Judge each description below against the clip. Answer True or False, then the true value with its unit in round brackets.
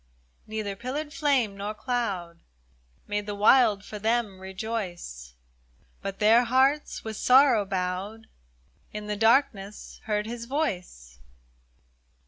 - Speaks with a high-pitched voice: True (210 Hz)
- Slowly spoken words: True (110 wpm)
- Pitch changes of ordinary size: True (3.5 semitones)